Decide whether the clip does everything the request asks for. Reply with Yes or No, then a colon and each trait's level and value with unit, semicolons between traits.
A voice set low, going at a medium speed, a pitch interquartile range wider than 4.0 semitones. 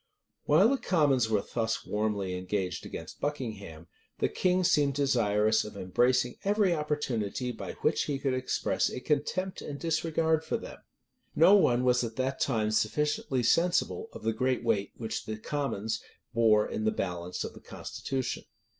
Yes: low, 125 Hz; average, 165 wpm; wide, 5.6 semitones